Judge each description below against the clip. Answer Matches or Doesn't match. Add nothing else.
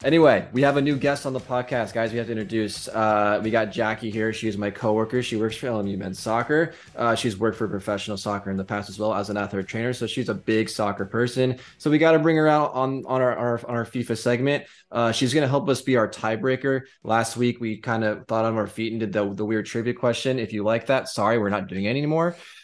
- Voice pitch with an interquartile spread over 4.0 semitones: Doesn't match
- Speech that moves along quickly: Matches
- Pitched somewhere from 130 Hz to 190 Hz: Doesn't match